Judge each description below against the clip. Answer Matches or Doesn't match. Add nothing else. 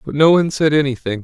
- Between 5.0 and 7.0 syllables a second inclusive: Doesn't match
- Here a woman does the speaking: Doesn't match